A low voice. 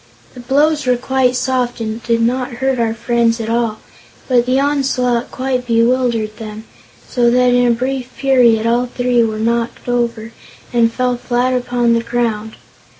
No: high, 240 Hz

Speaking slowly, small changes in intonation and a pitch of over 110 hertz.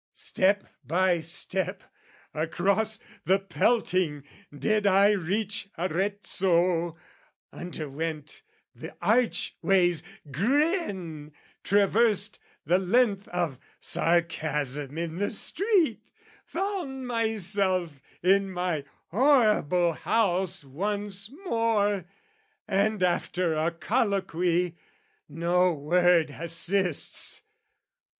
No: slow, 75 wpm; average, 3.6 semitones; medium, 185 Hz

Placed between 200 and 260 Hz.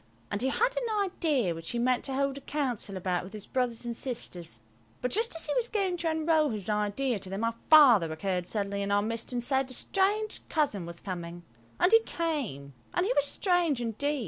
Yes: very high, 250 Hz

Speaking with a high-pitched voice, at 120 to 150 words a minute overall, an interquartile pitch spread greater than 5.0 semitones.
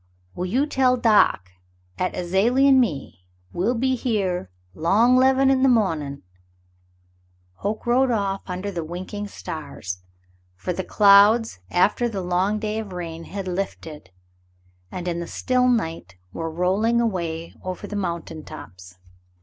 Yes: high, 195 Hz; average, 145 wpm; wide, 5.4 semitones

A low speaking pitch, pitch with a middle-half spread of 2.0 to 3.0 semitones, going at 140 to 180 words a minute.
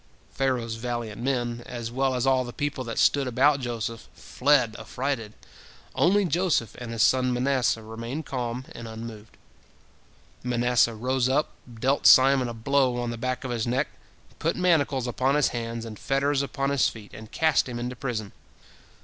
Yes: low, 125 Hz; average, 2.7 semitones; average, 165 wpm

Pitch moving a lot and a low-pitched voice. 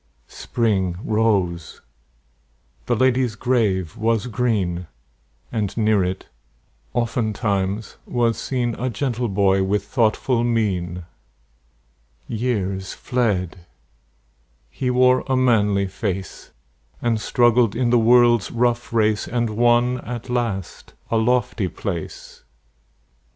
No: average, 3.7 semitones; low, 115 Hz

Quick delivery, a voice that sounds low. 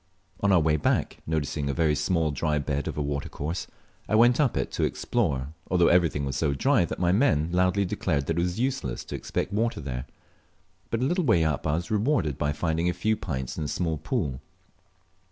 Yes: fast, 210 wpm; very low, 80 Hz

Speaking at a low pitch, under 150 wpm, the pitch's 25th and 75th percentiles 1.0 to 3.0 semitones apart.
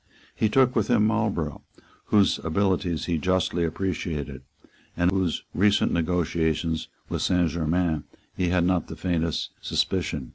Yes: very low, 90 Hz; average, 140 wpm; average, 2.7 semitones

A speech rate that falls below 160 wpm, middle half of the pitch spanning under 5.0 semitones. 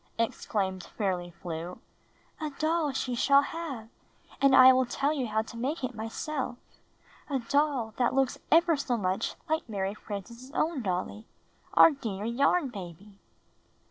No: average, 150 wpm; wide, 5.4 semitones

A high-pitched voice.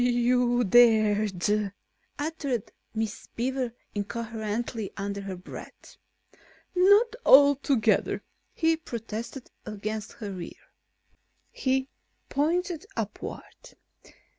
Yes: high, 240 Hz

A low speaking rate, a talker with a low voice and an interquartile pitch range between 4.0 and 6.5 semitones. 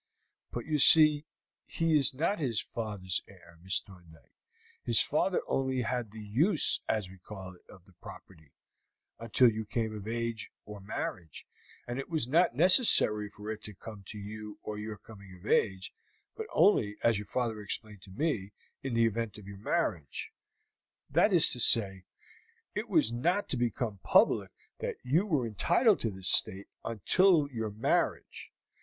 No: average, 165 wpm; low, 110 Hz; average, 4.9 semitones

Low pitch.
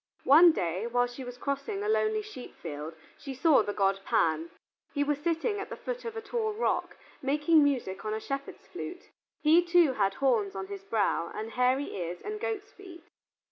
No: very high, 275 Hz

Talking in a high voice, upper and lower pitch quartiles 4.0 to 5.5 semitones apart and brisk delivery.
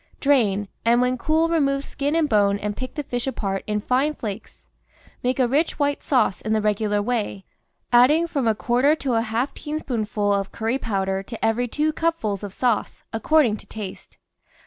No: high, 240 Hz; average, 5.1 semitones; average, 185 wpm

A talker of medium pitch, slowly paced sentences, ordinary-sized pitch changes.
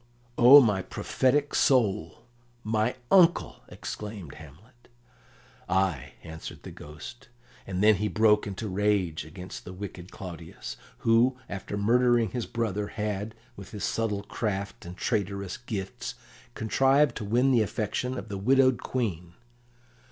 No: low, 105 Hz; slow, 130 wpm; average, 3.9 semitones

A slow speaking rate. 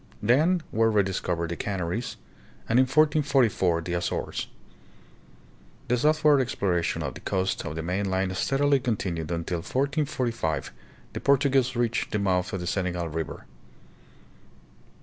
Yes: slow, 130 wpm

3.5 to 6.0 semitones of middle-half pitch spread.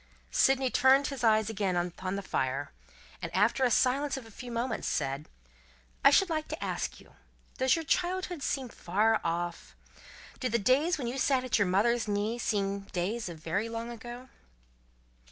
Yes: average, 4.9 semitones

